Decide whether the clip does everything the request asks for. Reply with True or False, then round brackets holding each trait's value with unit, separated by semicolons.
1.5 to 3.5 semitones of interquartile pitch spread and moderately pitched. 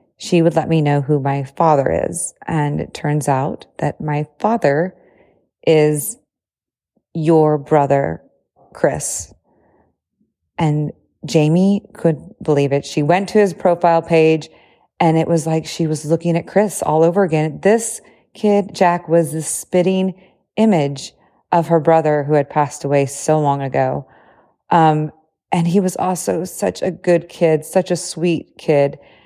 True (3.1 semitones; 165 Hz)